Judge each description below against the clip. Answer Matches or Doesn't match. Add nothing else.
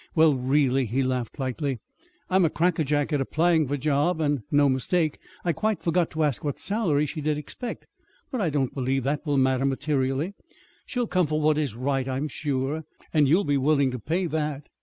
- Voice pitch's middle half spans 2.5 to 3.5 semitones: Matches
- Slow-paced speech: Doesn't match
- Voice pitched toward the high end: Doesn't match